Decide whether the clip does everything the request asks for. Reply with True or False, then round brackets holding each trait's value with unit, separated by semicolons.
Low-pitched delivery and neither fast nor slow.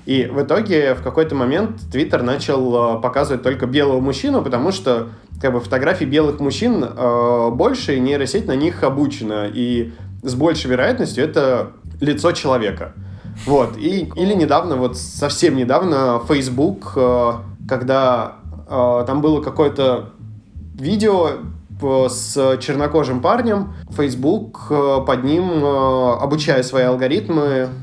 True (130 Hz; 125 wpm)